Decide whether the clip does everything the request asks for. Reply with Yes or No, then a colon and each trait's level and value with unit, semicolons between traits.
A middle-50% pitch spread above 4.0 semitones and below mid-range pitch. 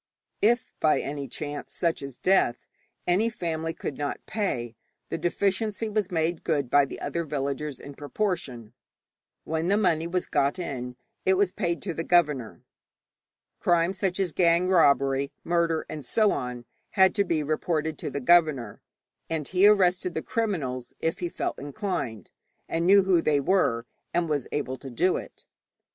No: average, 4.8 semitones; medium, 165 Hz